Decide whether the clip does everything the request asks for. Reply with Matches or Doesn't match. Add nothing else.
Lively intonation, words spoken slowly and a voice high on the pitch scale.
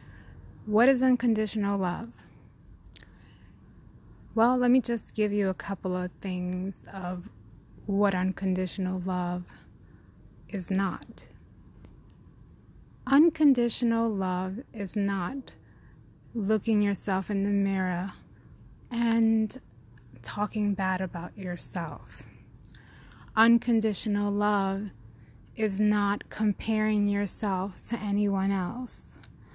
Doesn't match